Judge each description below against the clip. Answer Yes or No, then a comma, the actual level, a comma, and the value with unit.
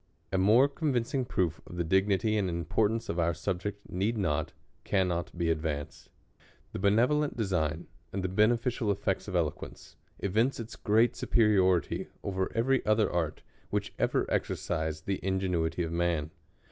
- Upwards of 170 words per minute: No, average, 145 wpm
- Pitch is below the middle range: Yes, very low, 95 Hz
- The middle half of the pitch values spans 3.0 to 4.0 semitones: No, average, 4.5 semitones